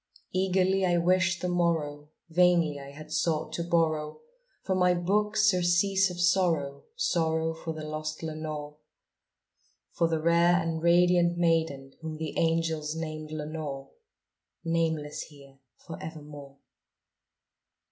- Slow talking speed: Yes, slow, 125 wpm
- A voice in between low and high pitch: Yes, medium, 165 Hz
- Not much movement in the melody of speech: Yes, narrow, 2.3 semitones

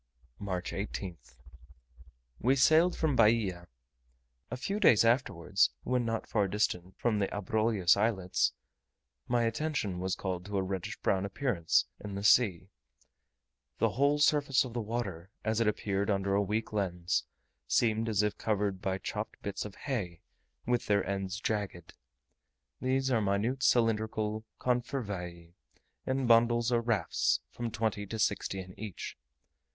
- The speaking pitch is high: No, low, 105 Hz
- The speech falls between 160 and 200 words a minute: No, average, 145 wpm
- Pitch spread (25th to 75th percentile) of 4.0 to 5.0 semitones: No, average, 3.4 semitones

